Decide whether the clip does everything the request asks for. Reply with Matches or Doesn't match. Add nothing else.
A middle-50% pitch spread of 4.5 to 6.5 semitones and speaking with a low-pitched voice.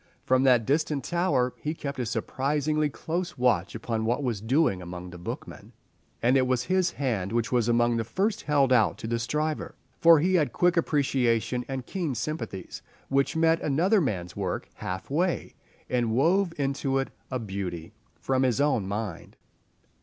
Matches